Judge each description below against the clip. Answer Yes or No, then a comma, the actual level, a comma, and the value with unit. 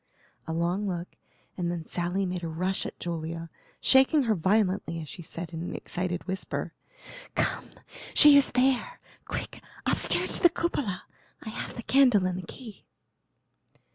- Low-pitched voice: No, medium, 185 Hz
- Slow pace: No, average, 160 wpm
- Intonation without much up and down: No, average, 5.3 semitones